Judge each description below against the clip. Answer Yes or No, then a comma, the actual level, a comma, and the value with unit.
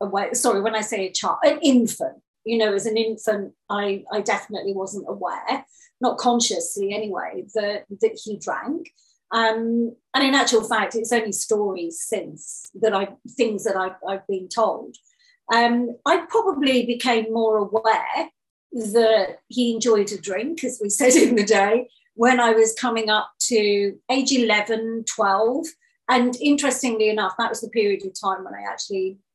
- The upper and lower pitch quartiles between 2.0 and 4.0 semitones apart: Yes, average, 3.2 semitones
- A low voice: No, high, 225 Hz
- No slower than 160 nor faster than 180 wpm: Yes, average, 165 wpm